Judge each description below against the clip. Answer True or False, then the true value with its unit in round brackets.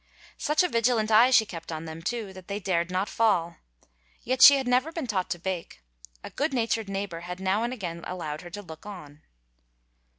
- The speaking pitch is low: False (195 Hz)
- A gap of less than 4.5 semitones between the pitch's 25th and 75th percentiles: False (5.2 semitones)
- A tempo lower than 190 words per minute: False (205 wpm)